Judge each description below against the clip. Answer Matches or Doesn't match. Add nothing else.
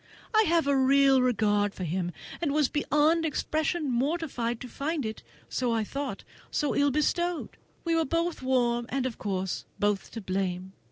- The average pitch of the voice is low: Doesn't match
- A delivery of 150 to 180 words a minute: Matches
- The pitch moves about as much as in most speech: Doesn't match